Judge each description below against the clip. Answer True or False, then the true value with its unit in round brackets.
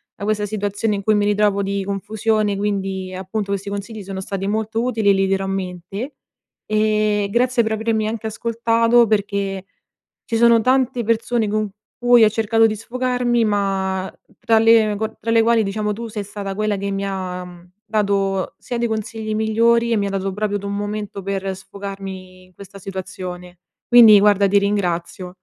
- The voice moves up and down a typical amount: False (2.3 semitones)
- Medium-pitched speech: False (205 Hz)